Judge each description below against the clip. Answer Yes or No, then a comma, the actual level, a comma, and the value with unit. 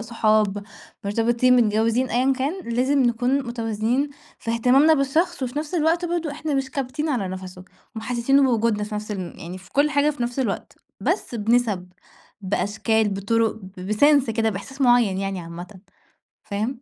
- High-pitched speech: Yes, high, 235 Hz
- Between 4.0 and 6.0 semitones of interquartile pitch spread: Yes, average, 4.6 semitones